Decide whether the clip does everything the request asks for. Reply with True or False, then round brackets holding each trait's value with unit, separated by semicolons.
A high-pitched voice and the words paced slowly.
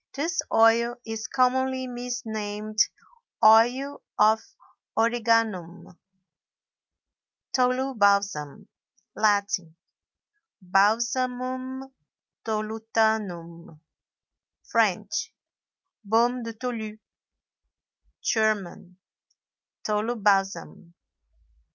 True (220 Hz; 45 wpm)